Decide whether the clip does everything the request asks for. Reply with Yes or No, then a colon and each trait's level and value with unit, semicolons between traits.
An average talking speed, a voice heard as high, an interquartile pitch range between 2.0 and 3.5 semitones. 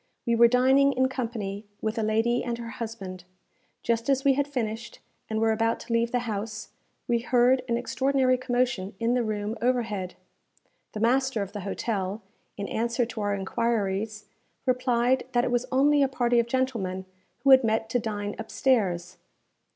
Yes: average, 175 wpm; high, 235 Hz; average, 2.9 semitones